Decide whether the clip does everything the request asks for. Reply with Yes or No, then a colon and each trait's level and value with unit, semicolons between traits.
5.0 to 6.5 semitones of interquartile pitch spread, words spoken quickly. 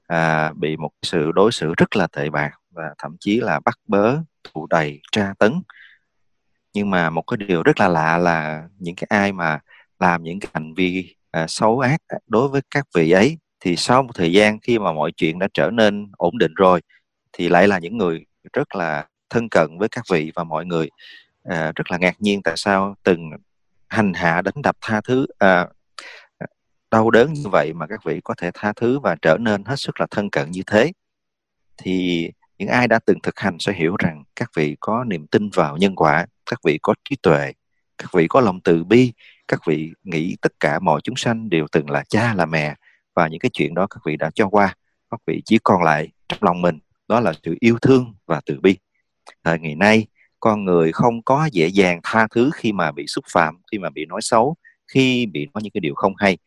Yes: wide, 5.5 semitones; fast, 225 wpm